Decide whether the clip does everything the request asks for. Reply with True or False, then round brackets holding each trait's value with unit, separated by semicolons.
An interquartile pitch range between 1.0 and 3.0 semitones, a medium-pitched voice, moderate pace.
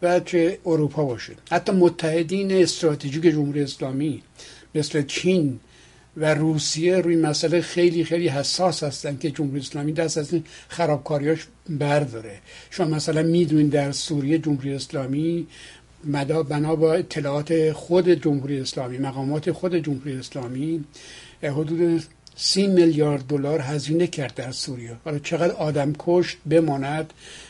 True (2.7 semitones; 155 Hz; 125 wpm)